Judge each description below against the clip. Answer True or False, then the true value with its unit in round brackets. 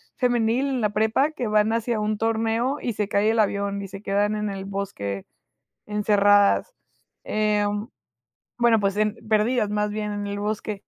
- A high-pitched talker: True (210 Hz)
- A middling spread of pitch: False (1.7 semitones)